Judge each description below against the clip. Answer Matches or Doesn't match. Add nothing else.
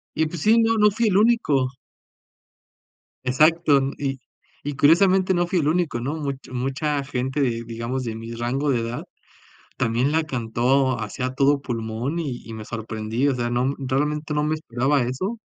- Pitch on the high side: Doesn't match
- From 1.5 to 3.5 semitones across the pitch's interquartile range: Doesn't match